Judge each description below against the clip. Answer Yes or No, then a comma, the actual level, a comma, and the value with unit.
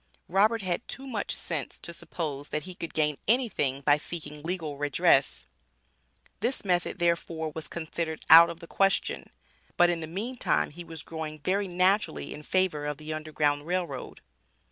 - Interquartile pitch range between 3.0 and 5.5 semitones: Yes, average, 3.4 semitones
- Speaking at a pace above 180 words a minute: No, average, 165 wpm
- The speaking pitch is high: No, medium, 165 Hz